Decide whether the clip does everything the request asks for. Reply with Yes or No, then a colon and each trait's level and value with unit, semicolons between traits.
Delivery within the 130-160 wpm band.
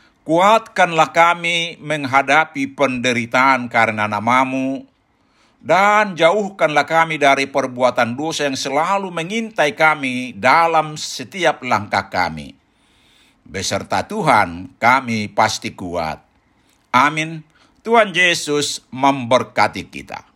No: average, 90 wpm